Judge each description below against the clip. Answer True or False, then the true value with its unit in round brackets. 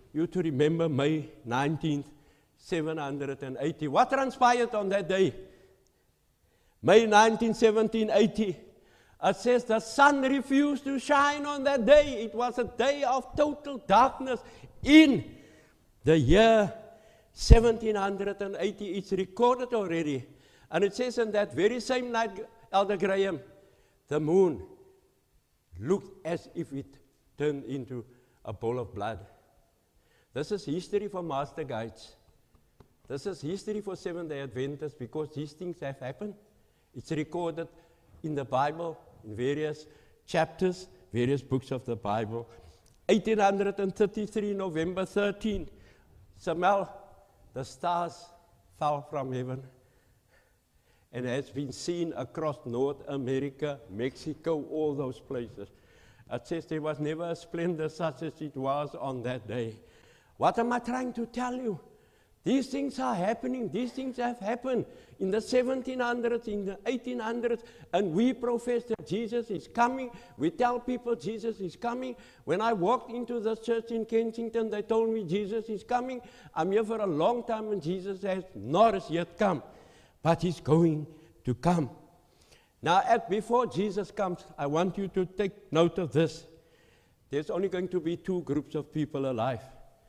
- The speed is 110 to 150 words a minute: True (140 wpm)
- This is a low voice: False (180 Hz)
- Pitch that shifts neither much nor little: False (7.7 semitones)